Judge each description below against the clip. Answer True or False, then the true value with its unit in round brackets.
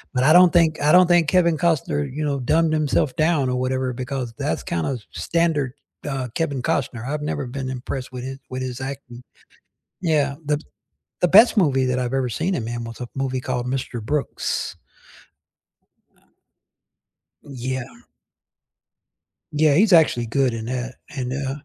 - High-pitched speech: False (135 Hz)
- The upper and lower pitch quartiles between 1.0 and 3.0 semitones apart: False (3.5 semitones)